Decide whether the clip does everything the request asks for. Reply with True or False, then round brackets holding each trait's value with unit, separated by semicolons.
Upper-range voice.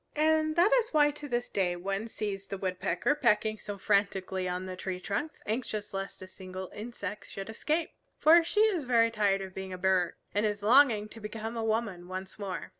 True (210 Hz)